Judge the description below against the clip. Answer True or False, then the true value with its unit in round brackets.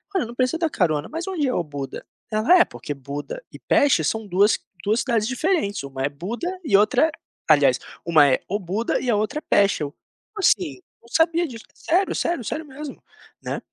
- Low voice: False (225 Hz)